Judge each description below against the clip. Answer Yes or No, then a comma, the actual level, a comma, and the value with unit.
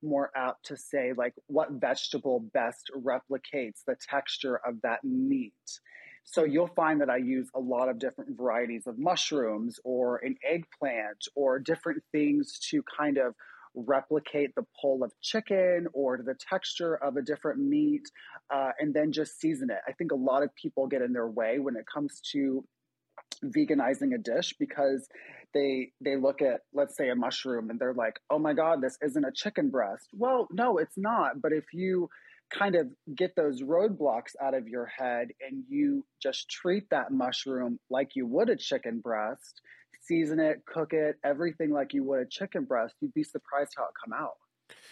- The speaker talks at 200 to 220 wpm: No, average, 185 wpm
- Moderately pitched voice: Yes, medium, 150 Hz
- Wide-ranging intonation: Yes, wide, 7.2 semitones